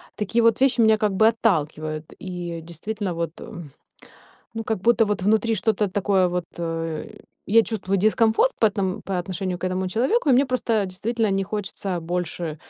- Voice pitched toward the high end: Yes, high, 195 Hz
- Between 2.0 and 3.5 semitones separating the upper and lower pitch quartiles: No, average, 3.9 semitones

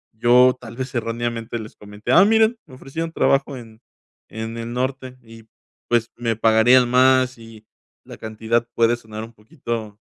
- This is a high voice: No, low, 120 Hz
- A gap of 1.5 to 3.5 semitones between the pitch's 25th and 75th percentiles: Yes, narrow, 2.4 semitones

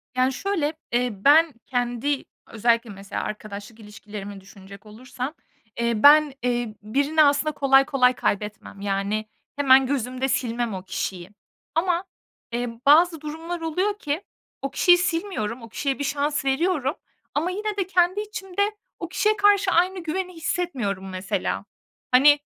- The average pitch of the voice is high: Yes, very high, 275 Hz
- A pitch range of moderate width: No, wide, 6.8 semitones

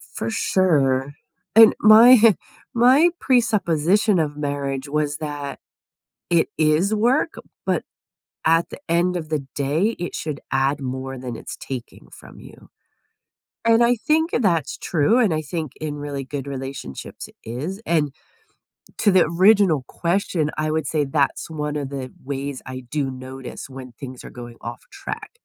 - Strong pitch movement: Yes, wide, 5.7 semitones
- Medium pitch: Yes, medium, 150 Hz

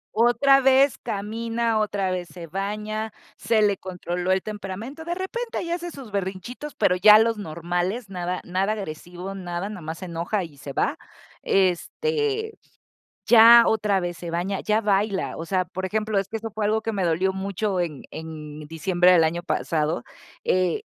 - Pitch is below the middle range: No, high, 195 Hz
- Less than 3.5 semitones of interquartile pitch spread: No, average, 3.9 semitones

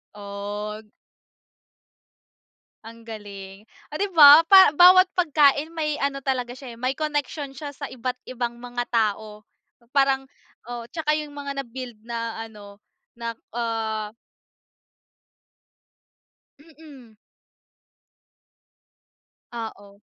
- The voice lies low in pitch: No, very high, 250 Hz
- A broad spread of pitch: No, average, 4.6 semitones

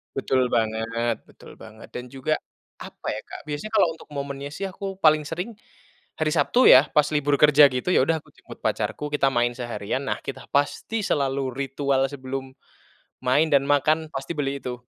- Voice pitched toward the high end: No, medium, 140 Hz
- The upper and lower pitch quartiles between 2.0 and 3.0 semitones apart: Yes, average, 2.7 semitones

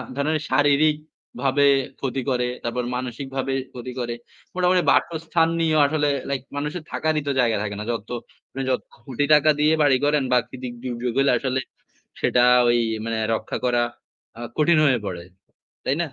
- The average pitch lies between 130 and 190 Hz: Yes, low, 135 Hz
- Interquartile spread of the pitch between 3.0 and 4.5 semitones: Yes, average, 3.6 semitones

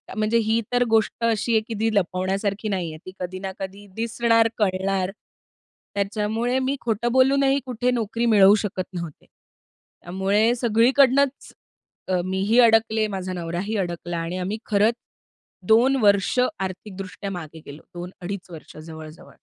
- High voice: Yes, high, 205 Hz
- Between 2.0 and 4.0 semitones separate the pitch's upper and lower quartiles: Yes, average, 3.7 semitones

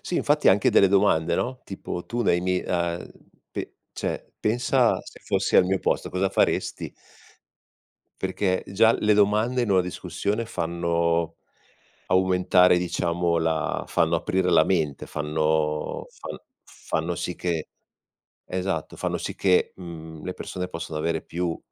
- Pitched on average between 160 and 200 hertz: No, very low, 90 Hz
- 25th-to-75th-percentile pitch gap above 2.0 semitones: Yes, narrow, 2.6 semitones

